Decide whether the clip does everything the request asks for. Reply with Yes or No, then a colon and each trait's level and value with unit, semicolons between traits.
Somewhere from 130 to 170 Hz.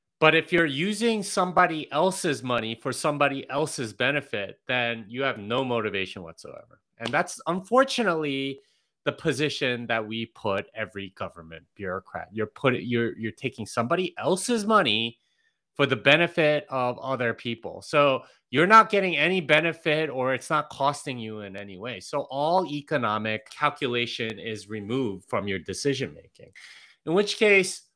Yes: low, 135 Hz